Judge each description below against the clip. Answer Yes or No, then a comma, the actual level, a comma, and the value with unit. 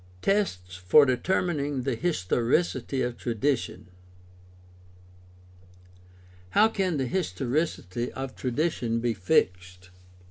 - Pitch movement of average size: No, wide, 8.0 semitones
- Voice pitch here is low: Yes, low, 120 Hz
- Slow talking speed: Yes, slow, 95 wpm